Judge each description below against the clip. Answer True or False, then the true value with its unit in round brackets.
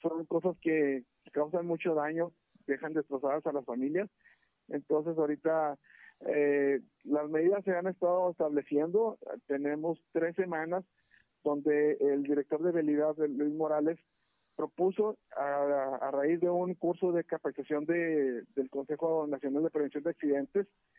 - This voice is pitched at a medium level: True (155 Hz)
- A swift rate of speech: False (135 wpm)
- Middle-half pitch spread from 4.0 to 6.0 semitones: False (2.8 semitones)